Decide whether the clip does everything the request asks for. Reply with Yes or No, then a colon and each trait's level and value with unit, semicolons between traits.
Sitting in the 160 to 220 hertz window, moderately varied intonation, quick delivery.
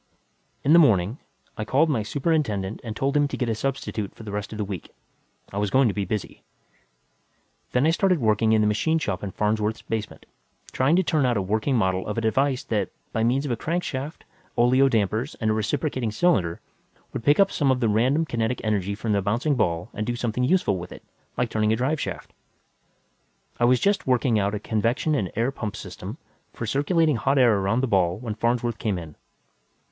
No: low, 115 Hz; average, 4.5 semitones; fast, 210 wpm